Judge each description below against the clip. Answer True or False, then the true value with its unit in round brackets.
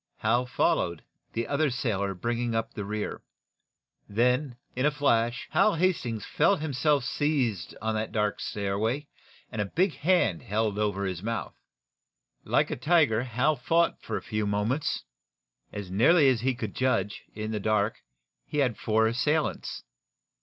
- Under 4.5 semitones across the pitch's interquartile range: False (4.9 semitones)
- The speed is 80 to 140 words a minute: False (155 wpm)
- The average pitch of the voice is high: False (115 Hz)